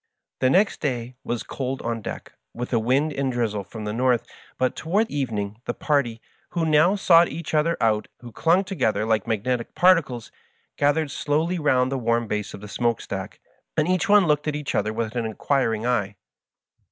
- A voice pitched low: Yes, low, 130 Hz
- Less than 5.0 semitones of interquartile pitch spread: No, average, 5.3 semitones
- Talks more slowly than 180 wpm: No, average, 190 wpm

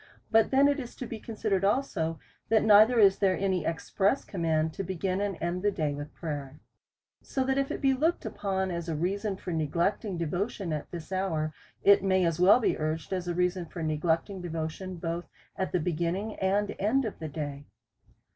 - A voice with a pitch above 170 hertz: Yes, medium, 185 Hz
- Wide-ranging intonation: No, average, 3.9 semitones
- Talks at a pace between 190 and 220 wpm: Yes, average, 195 wpm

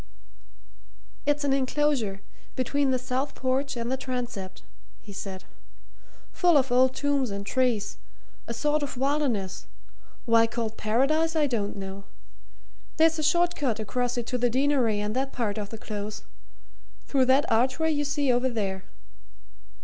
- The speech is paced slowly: No, average, 150 wpm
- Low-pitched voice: No, very high, 255 Hz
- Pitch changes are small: No, average, 4.5 semitones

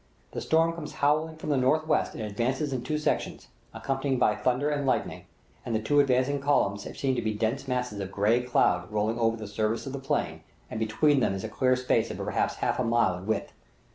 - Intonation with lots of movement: No, average, 4.5 semitones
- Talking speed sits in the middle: No, fast, 215 wpm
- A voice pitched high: No, low, 125 Hz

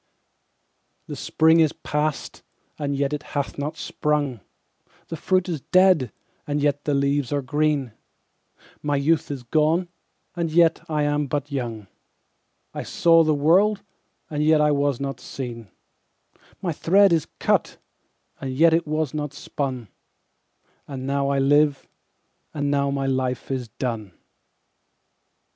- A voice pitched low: No, medium, 145 Hz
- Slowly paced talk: Yes, slow, 130 wpm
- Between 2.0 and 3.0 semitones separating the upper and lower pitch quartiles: Yes, narrow, 2.4 semitones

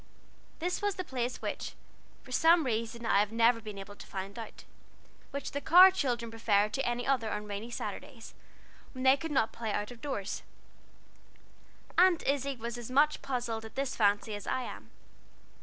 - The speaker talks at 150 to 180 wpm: Yes, average, 175 wpm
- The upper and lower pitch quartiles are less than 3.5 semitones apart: No, average, 4.0 semitones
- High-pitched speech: Yes, high, 240 Hz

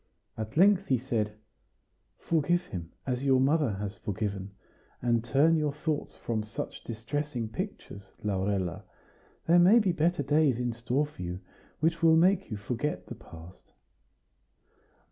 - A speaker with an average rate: Yes, average, 145 wpm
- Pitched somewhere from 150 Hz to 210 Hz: No, low, 130 Hz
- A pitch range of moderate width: No, wide, 7.1 semitones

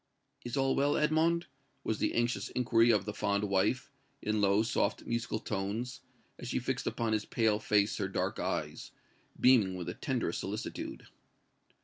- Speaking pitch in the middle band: No, low, 115 Hz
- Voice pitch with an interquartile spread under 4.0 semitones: Yes, average, 3.5 semitones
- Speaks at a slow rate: No, average, 160 wpm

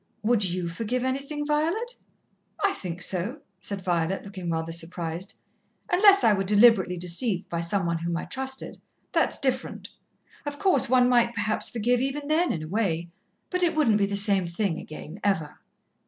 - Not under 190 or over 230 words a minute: No, average, 170 wpm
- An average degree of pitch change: No, wide, 7.2 semitones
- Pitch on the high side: Yes, high, 205 Hz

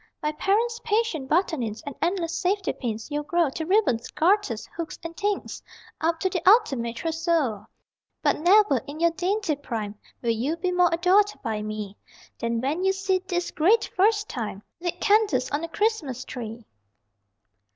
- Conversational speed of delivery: Yes, average, 160 wpm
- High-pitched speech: Yes, very high, 330 Hz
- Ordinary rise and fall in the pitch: No, wide, 7.1 semitones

